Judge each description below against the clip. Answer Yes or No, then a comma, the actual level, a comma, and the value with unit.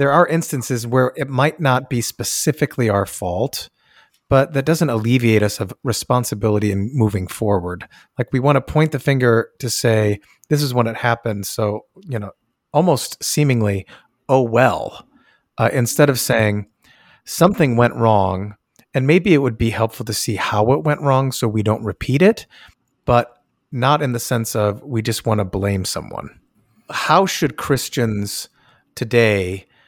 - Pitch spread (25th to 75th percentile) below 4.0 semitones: No, average, 4.5 semitones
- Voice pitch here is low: Yes, low, 120 Hz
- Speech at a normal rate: Yes, average, 165 wpm